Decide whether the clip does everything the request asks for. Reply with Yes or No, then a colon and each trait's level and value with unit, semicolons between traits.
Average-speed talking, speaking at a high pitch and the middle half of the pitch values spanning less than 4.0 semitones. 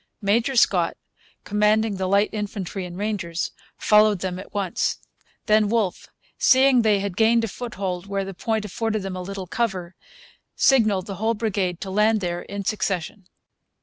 Yes: average, 160 wpm; high, 200 Hz; narrow, 2.5 semitones